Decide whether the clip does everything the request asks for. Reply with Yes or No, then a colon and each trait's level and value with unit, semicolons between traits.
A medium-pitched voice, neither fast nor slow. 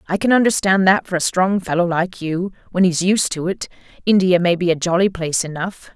No: medium, 180 Hz; fast, 220 wpm